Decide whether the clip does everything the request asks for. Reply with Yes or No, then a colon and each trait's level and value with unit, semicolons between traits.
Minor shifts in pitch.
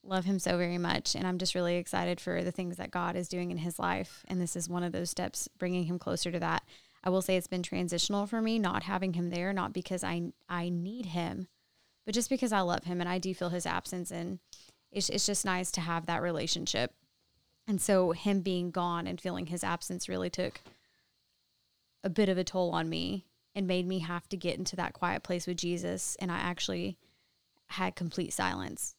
Yes: narrow, 1.3 semitones